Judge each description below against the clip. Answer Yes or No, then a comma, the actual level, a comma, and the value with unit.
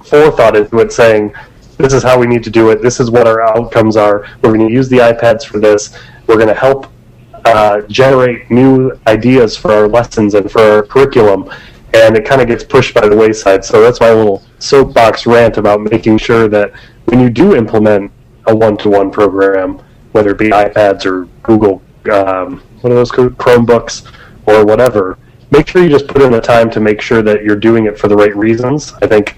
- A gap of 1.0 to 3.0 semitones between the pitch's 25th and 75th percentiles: Yes, narrow, 2.6 semitones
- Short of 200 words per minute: No, fast, 205 wpm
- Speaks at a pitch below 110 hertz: No, low, 115 Hz